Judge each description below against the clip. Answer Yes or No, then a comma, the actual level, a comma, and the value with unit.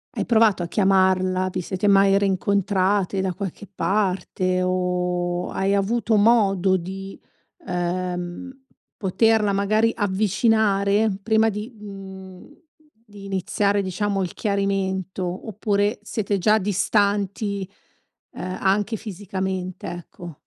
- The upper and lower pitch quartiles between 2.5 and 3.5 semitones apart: No, narrow, 1.9 semitones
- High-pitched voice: Yes, high, 195 Hz